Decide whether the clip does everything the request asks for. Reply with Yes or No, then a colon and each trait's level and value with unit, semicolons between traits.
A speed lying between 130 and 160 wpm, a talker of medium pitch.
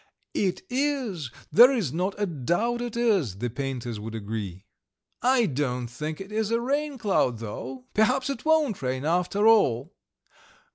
Yes: average, 155 wpm; medium, 180 Hz